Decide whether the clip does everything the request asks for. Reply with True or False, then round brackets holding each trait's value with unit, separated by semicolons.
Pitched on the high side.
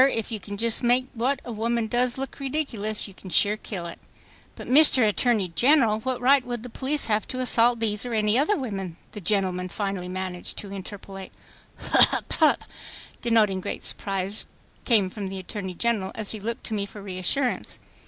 True (215 Hz)